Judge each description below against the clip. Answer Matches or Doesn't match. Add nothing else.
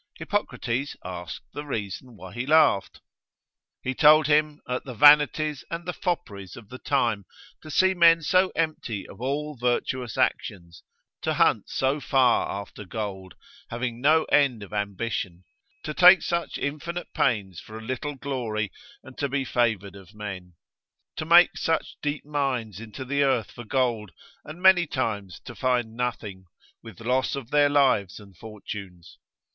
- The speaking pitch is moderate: Doesn't match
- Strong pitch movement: Matches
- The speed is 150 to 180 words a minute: Matches